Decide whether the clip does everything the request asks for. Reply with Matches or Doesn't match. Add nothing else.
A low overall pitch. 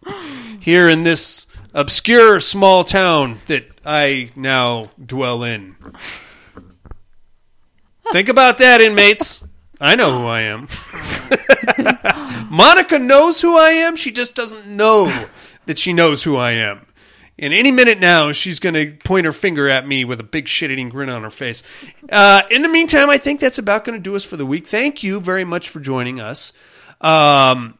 Doesn't match